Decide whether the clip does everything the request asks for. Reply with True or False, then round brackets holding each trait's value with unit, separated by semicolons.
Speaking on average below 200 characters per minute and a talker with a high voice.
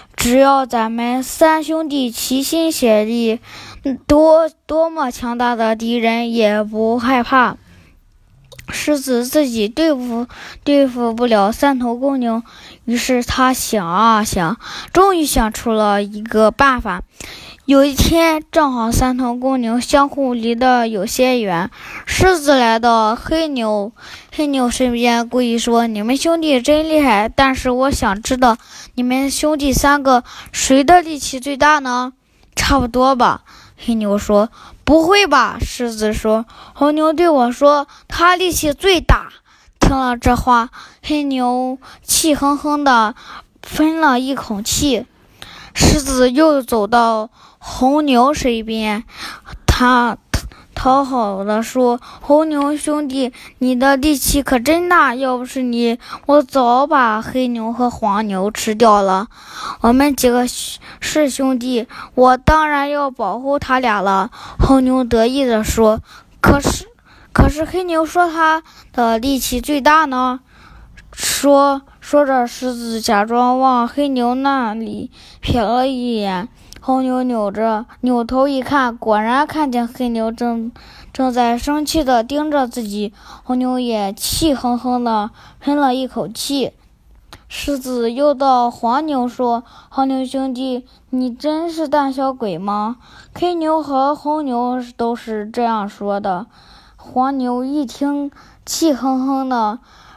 True (185 characters per minute; 255 Hz)